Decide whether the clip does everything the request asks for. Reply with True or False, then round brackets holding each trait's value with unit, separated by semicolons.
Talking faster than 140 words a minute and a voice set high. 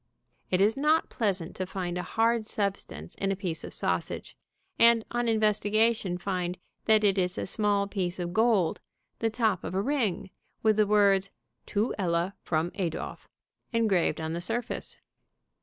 True (160 wpm; 200 Hz)